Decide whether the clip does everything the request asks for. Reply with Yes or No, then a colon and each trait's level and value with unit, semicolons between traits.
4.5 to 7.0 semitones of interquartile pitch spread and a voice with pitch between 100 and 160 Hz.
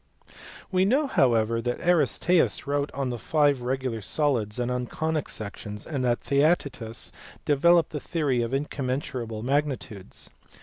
No: average, 4.1 semitones; low, 135 Hz